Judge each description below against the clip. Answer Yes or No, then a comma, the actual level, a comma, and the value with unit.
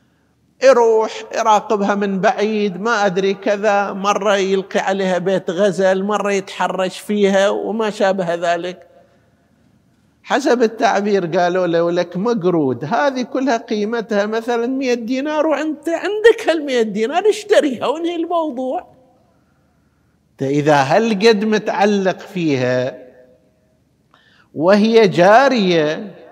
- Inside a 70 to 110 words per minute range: Yes, average, 100 wpm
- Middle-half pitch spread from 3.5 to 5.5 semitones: Yes, average, 3.9 semitones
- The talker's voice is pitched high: Yes, high, 205 Hz